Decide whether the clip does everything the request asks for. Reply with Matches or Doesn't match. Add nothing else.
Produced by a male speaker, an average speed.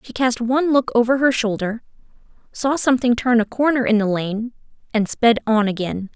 Doesn't match